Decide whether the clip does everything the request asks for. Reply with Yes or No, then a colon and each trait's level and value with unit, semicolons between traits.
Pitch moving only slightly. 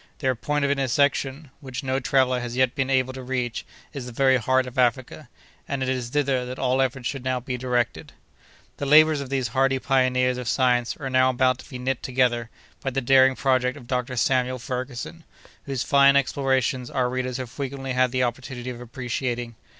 Yes: narrow, 1.2 semitones